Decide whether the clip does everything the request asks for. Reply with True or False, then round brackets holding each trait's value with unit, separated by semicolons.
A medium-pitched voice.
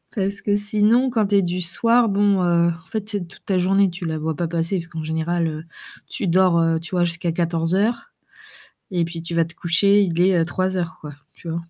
True (175 Hz)